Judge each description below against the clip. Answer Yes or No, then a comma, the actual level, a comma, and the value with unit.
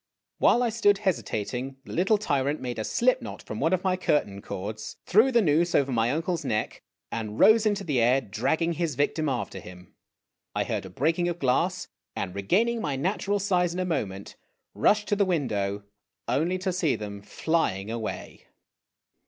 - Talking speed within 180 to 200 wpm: Yes, average, 185 wpm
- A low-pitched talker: No, medium, 155 Hz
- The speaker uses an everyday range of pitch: No, wide, 8.8 semitones